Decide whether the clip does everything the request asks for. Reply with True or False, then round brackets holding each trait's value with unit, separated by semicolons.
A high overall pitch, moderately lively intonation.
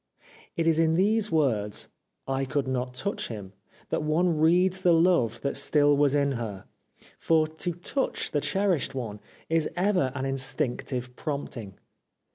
False (145 Hz; 4.7 semitones)